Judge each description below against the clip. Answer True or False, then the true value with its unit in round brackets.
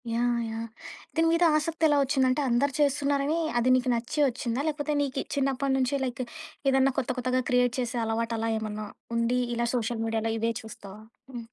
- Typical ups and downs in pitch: True (3.2 semitones)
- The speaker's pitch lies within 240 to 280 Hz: True (250 Hz)